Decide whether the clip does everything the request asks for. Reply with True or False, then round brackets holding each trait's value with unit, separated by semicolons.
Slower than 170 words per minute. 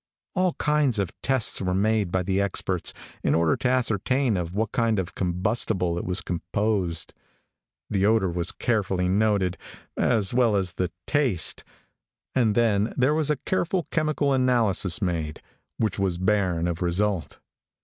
True (150 wpm)